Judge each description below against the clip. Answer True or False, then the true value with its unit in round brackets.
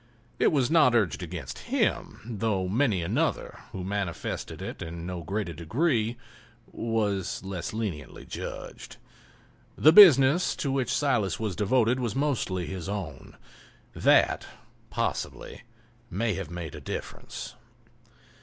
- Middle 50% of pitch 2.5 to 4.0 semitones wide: False (5.3 semitones)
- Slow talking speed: True (120 wpm)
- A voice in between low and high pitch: False (105 Hz)